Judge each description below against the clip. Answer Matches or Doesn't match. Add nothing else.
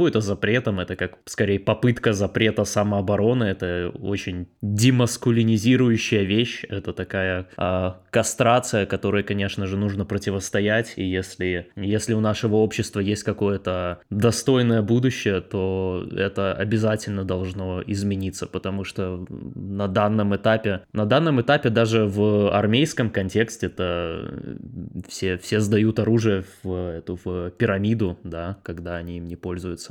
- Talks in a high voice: Doesn't match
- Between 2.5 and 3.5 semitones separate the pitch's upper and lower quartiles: Matches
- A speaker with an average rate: Matches